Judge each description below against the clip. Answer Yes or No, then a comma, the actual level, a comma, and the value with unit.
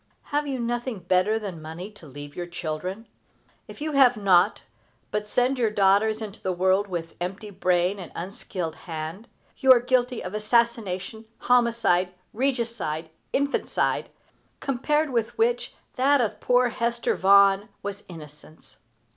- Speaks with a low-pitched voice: No, high, 210 Hz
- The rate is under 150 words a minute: Yes, average, 140 wpm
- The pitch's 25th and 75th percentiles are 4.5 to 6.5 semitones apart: Yes, average, 5.1 semitones